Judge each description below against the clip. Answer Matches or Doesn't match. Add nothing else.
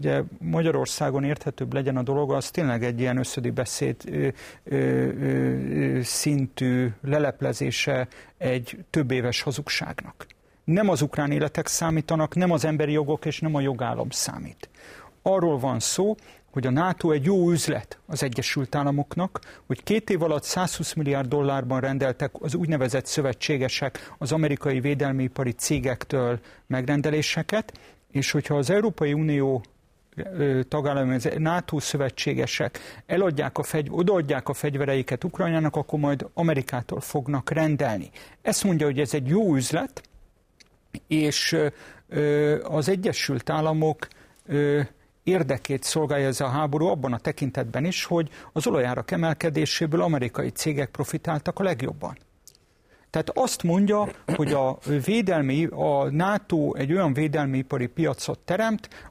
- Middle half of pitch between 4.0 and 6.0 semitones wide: Doesn't match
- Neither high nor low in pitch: Matches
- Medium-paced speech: Matches